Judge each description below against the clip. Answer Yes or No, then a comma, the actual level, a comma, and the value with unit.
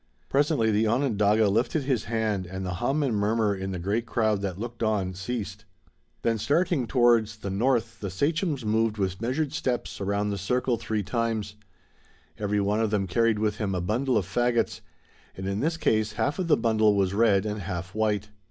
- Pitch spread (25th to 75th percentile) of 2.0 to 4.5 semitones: Yes, average, 3.0 semitones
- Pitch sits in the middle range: No, low, 110 Hz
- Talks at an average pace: Yes, average, 190 wpm